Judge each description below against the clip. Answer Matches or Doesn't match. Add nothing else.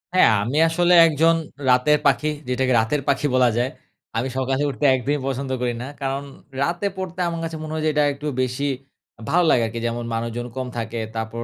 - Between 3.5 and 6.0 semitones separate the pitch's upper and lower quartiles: Matches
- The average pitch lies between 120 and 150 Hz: Matches